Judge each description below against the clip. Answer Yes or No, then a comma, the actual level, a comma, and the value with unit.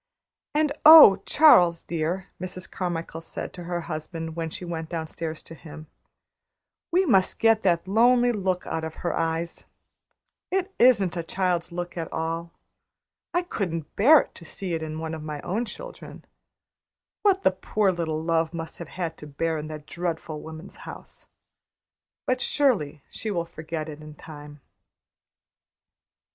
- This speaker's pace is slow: No, average, 155 wpm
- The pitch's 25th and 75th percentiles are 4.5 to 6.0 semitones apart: No, average, 3.3 semitones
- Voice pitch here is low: No, medium, 170 Hz